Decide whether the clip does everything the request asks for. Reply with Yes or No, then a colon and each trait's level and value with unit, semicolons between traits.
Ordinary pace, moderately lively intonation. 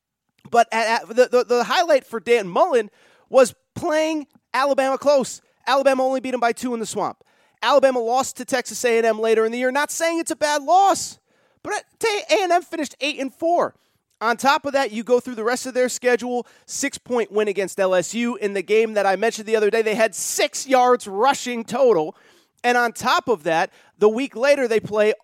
No: fast, 215 wpm; average, 3.6 semitones